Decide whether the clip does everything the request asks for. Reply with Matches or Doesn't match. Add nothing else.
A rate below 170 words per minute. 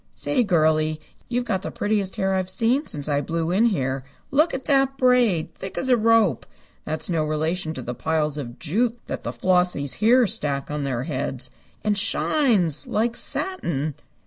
Doesn't match